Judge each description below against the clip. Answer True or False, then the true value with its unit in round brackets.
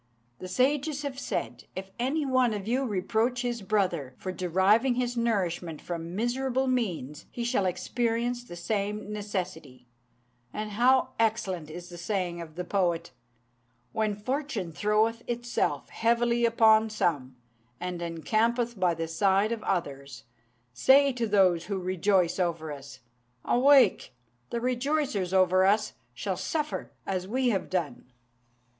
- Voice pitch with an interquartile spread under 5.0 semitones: False (5.3 semitones)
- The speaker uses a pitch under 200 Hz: False (210 Hz)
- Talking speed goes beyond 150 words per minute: False (140 wpm)